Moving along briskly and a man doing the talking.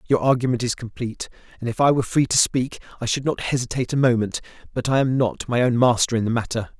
Yes: fast, 240 wpm; male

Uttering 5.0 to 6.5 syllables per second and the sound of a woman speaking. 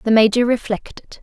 Yes: 5.4 syllables/s; female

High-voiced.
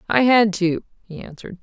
Yes: high, 200 Hz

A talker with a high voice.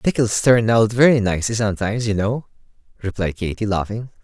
No: low, 105 Hz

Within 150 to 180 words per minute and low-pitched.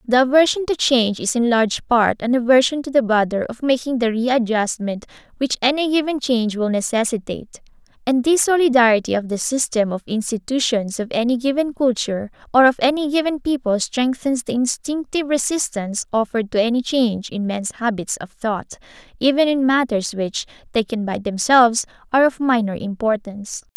No: average, 160 wpm; high, 245 Hz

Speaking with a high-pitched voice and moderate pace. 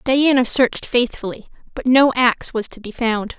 Yes: high, 240 Hz; average, 175 wpm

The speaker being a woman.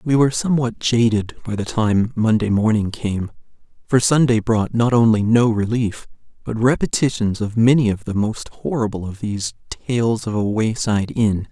No: male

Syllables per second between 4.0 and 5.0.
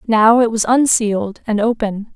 Yes: 4.5 syllables/s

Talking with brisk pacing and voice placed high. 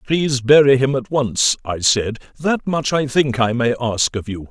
No: fast, 215 wpm; low, 130 Hz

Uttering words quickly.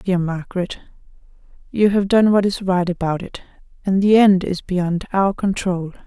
No: average, 170 wpm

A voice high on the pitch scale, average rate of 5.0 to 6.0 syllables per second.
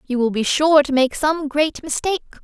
Yes: very high, 290 Hz; 5.4 syllables/s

